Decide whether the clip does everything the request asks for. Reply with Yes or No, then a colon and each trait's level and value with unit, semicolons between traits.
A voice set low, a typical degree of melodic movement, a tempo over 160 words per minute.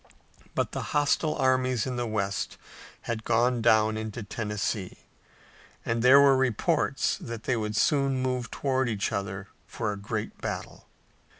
No: low, 115 Hz; average, 3.3 semitones; average, 145 wpm